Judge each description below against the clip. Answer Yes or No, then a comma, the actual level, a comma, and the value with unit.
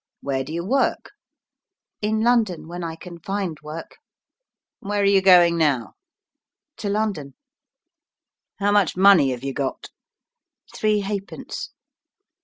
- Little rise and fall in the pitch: No, average, 4.6 semitones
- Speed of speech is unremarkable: No, slow, 125 wpm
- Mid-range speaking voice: Yes, medium, 180 Hz